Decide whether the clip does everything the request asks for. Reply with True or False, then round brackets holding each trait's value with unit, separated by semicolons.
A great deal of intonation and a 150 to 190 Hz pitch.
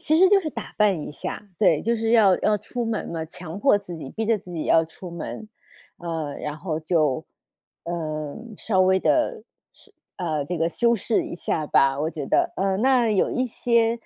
True (5.9 semitones; 185 Hz)